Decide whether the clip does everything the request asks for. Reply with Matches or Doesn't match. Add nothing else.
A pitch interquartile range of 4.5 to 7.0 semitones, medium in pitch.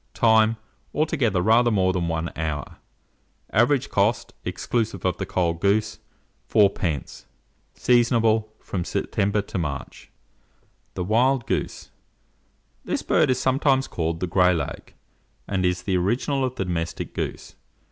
Doesn't match